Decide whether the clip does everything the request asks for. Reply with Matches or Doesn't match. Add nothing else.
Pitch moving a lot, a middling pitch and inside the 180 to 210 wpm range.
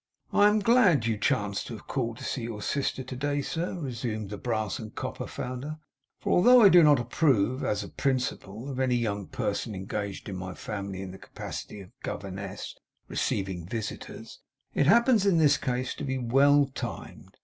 Doesn't match